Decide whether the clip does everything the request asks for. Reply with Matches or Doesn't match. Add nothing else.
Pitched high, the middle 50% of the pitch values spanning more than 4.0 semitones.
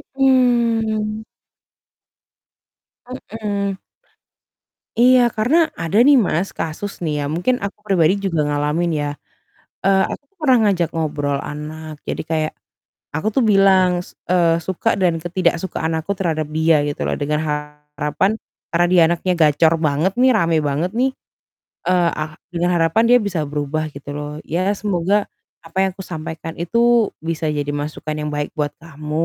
Doesn't match